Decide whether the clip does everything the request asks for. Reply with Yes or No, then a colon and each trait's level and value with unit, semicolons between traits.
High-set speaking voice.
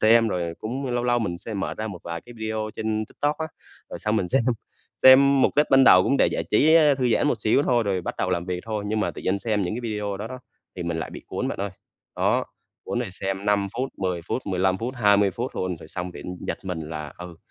No: low, 105 Hz